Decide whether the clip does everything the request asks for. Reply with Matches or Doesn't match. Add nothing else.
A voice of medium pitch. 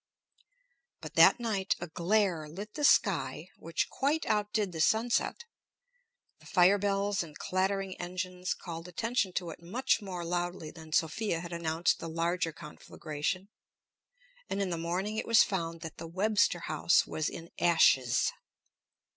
Matches